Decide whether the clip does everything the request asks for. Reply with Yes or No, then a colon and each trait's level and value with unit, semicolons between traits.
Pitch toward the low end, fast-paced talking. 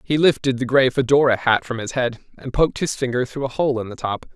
Yes: low, 130 Hz; fast, 260 wpm